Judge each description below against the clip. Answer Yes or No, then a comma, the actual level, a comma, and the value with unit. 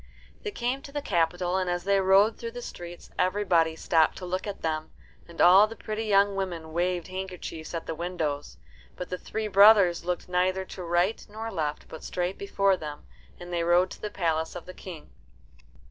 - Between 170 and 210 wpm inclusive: Yes, average, 195 wpm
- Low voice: No, medium, 180 Hz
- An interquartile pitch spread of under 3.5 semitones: Yes, average, 2.7 semitones